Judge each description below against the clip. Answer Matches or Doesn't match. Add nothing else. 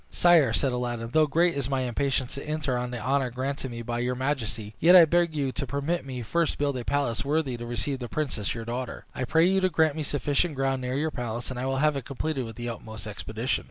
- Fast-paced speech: Matches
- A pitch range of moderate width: Matches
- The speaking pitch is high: Doesn't match